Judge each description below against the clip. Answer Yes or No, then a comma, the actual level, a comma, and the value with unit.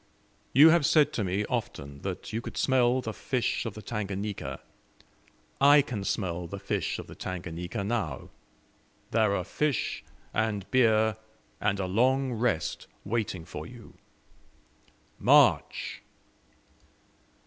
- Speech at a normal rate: No, slow, 125 wpm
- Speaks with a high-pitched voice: No, low, 110 Hz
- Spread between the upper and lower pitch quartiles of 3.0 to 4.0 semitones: No, average, 4.5 semitones